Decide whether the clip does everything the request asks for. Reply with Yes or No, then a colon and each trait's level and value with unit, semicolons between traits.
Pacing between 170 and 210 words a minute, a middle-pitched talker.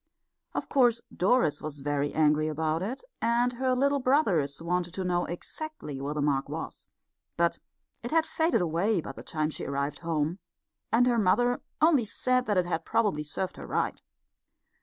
Yes: average, 175 wpm; medium, 180 Hz